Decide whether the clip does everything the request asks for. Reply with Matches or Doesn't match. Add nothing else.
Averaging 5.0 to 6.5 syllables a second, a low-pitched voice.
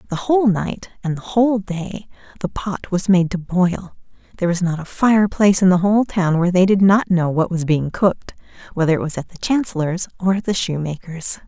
Doesn't match